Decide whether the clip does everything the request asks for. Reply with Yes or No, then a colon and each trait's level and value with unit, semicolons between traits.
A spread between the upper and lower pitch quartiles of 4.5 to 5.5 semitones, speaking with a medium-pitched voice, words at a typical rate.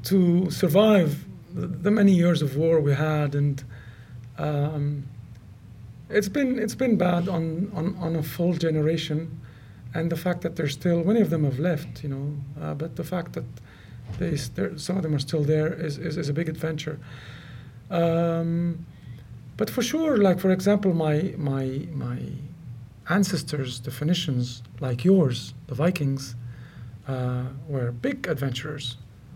Yes: average, 5.0 semitones; medium, 150 Hz; average, 150 wpm